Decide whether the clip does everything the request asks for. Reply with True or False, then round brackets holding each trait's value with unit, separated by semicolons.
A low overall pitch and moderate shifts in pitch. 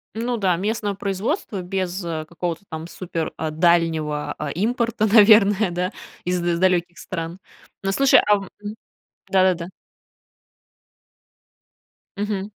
False (185 Hz; 3.3 semitones)